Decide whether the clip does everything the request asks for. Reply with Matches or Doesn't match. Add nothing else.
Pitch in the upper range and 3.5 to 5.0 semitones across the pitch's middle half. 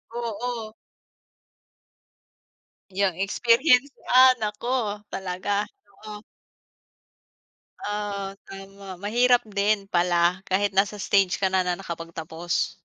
Doesn't match